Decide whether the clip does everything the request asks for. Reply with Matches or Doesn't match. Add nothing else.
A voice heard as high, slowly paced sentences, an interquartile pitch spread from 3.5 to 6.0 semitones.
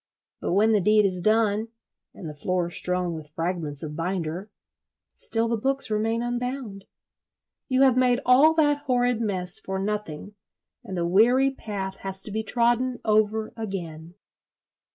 Doesn't match